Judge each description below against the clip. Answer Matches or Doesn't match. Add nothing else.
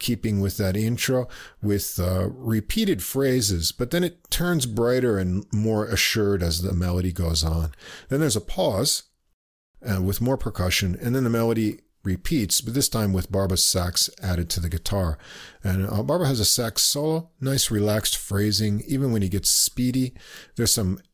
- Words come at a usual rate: Matches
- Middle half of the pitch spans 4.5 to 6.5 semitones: Matches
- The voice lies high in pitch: Doesn't match